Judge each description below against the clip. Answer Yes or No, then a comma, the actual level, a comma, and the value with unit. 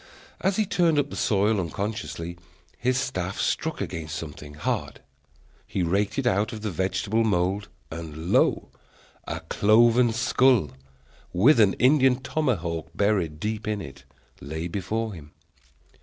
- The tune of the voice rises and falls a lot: Yes, wide, 5.8 semitones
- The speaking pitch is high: No, low, 105 Hz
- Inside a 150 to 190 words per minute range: No, average, 140 wpm